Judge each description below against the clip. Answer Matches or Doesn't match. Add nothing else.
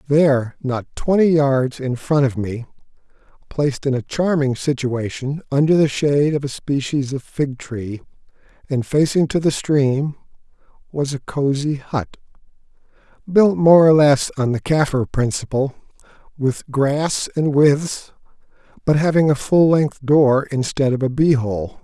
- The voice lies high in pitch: Doesn't match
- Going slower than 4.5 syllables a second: Matches